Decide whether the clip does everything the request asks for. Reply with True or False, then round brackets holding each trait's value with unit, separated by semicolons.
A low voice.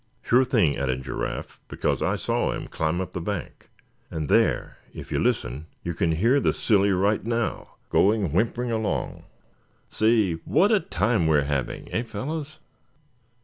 True (100 Hz)